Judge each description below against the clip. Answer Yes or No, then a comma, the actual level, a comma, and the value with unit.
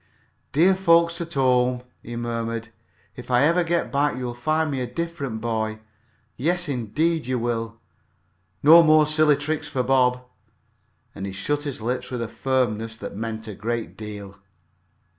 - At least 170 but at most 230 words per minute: No, average, 160 wpm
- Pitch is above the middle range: No, low, 125 Hz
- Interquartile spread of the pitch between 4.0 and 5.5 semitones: Yes, average, 5.2 semitones